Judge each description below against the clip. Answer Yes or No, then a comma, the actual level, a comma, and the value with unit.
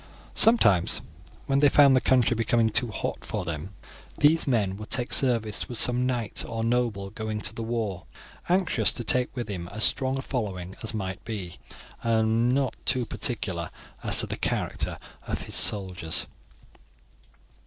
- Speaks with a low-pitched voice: Yes, low, 115 Hz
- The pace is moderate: Yes, average, 165 wpm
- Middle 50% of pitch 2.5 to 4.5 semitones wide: Yes, average, 3.8 semitones